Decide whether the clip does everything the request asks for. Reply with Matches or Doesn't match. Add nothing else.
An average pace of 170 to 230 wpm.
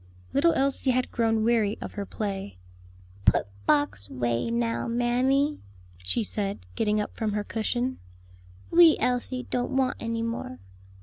Doesn't match